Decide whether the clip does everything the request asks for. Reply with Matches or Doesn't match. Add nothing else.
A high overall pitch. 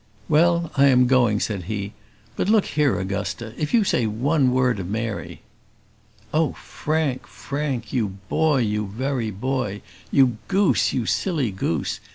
Doesn't match